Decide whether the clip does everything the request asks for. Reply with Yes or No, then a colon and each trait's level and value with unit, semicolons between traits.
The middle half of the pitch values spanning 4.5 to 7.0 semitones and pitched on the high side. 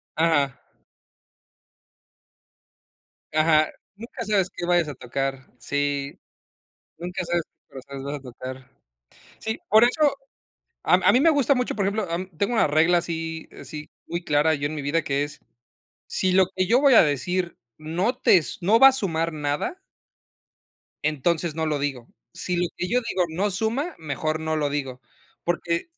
No: average, 4.9 semitones; medium, 165 Hz